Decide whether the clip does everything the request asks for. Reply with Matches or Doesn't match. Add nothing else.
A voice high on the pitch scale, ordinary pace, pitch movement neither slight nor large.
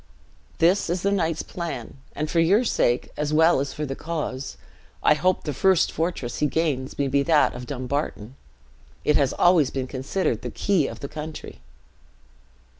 Doesn't match